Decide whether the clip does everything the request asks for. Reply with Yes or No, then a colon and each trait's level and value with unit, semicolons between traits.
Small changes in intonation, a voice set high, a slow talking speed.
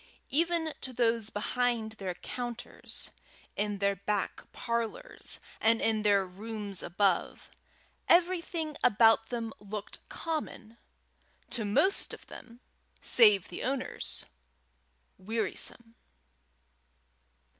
No: average, 3.3 semitones; high, 225 Hz; slow, 95 wpm